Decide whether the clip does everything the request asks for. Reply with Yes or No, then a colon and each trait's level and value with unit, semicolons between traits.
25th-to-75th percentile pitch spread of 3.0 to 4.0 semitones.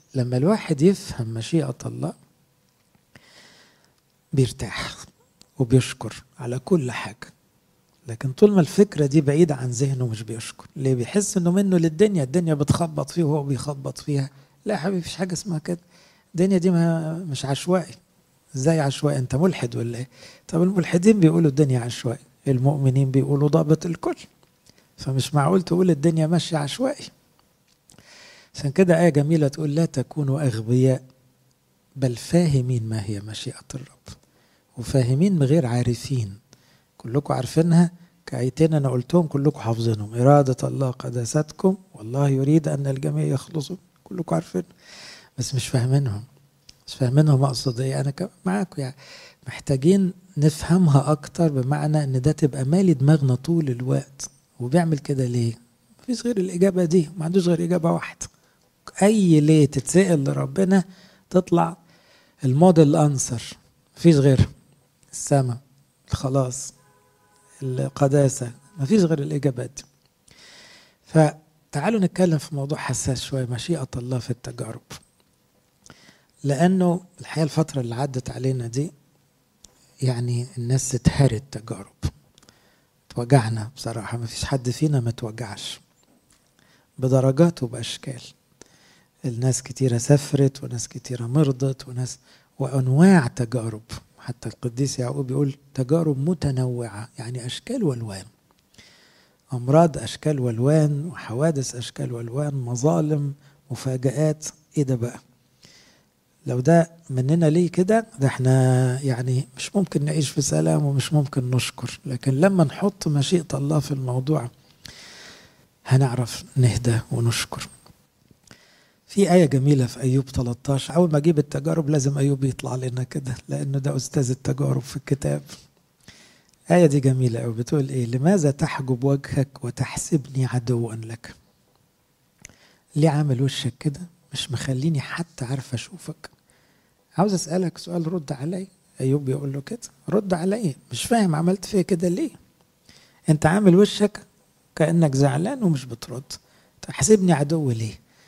No: average, 4.4 semitones